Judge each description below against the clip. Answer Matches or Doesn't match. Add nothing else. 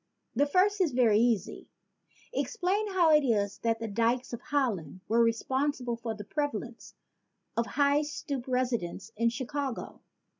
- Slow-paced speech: Doesn't match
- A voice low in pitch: Doesn't match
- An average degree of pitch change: Matches